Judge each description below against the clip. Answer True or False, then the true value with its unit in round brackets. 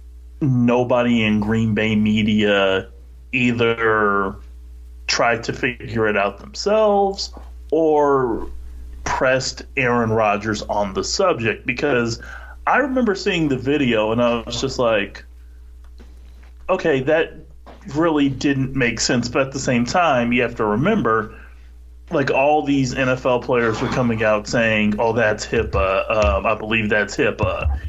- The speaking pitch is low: True (115 Hz)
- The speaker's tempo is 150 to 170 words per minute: False (135 wpm)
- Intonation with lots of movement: True (9.0 semitones)